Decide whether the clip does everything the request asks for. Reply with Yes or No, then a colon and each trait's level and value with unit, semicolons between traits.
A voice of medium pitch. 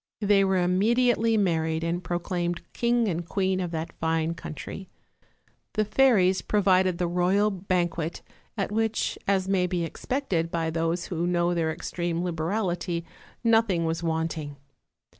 Yes: medium, 180 Hz